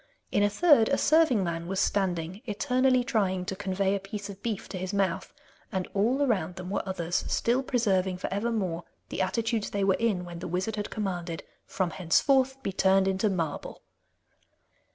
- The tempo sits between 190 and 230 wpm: No, average, 180 wpm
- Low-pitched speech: No, high, 195 Hz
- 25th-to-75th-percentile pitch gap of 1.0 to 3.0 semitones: No, average, 3.7 semitones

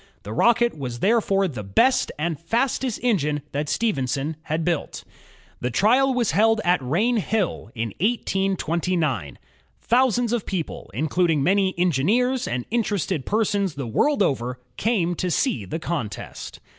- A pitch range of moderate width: No, wide, 7.8 semitones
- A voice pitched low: No, medium, 180 Hz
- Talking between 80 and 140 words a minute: Yes, slow, 135 wpm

